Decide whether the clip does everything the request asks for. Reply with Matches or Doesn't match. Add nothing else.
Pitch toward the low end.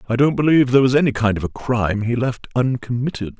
Matches